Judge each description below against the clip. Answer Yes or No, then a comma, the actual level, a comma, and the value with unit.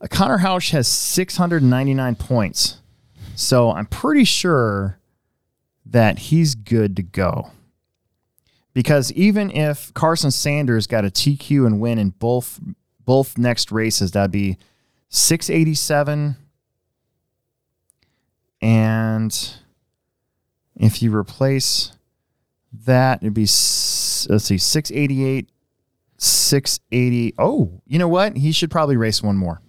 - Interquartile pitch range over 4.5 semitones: Yes, average, 5.1 semitones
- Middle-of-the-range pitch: No, low, 125 Hz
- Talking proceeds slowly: Yes, slow, 110 wpm